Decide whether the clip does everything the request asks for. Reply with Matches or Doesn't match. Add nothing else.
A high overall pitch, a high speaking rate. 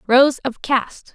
Doesn't match